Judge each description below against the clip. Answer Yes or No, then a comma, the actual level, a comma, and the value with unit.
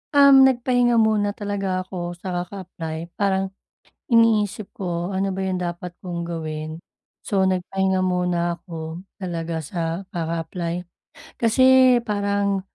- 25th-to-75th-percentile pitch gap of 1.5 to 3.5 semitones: Yes, average, 2.9 semitones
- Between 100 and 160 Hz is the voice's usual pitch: No, medium, 185 Hz